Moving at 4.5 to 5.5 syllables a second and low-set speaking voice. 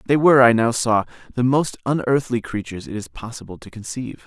No: 6.2 syllables/s; low, 120 Hz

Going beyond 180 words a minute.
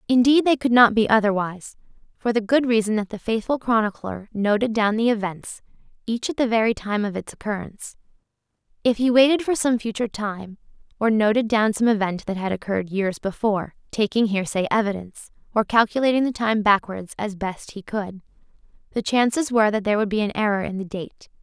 Yes: average, 190 wpm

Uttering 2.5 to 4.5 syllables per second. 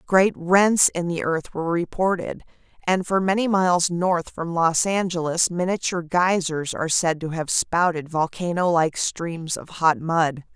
Yes: 4.4 syllables/s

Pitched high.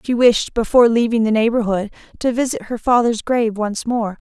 Yes: high, 230 Hz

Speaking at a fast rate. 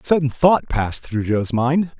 Yes: fast, 210 wpm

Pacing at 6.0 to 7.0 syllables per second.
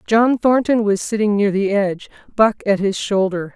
No: 4.8 syllables/s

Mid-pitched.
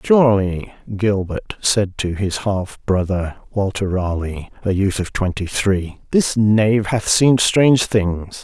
No: low, 100 Hz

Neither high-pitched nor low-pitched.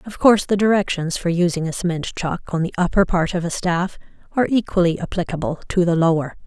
Yes: medium, 180 Hz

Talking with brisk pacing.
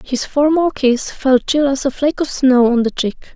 Yes: fast, 230 wpm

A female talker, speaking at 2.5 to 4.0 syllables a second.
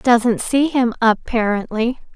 Yes: female; 3.7 syllables/s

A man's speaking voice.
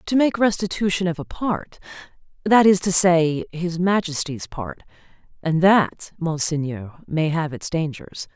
No: female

